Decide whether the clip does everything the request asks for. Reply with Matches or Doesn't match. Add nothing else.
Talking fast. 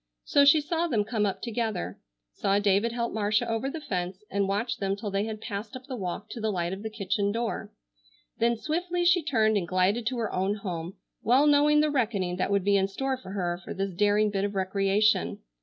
Matches